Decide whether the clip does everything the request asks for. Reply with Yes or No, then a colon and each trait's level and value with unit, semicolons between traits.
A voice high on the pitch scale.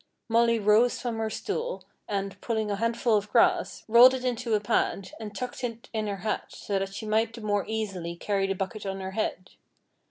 Yes: high, 215 Hz